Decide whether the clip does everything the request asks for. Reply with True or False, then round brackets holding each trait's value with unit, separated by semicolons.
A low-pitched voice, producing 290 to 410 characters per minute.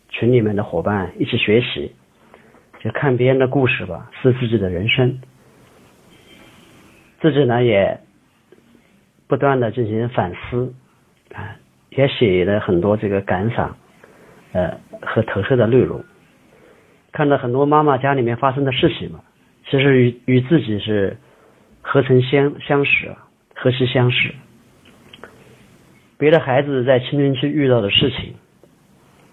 False (125 Hz; 195 characters per minute)